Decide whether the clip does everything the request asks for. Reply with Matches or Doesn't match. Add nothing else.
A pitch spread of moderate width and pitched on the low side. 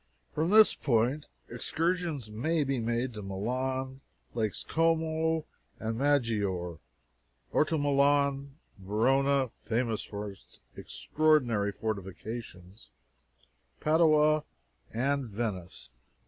Doesn't match